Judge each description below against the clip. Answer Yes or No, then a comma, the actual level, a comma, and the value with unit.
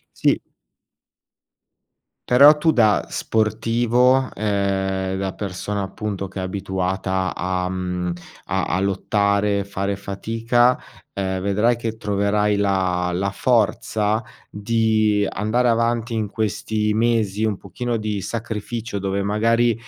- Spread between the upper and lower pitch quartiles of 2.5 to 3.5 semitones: Yes, average, 2.8 semitones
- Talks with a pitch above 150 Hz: No, low, 105 Hz